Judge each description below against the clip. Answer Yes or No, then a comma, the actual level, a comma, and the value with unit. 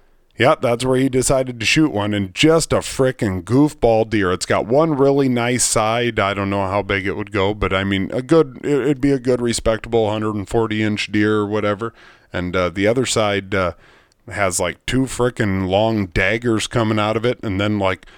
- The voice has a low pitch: Yes, low, 110 Hz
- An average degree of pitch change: Yes, average, 3.8 semitones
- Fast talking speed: Yes, fast, 210 wpm